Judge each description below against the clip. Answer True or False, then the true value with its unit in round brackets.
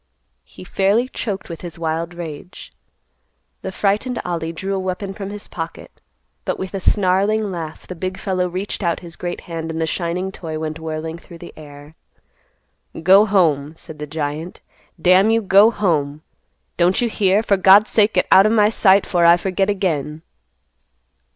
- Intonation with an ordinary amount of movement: True (3.4 semitones)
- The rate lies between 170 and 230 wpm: True (175 wpm)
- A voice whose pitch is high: False (180 Hz)